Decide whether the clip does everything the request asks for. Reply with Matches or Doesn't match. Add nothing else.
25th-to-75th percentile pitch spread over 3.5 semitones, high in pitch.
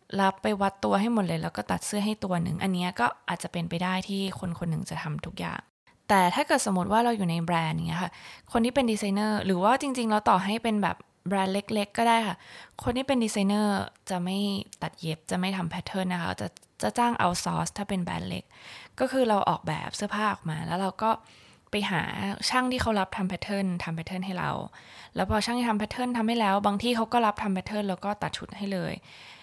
Doesn't match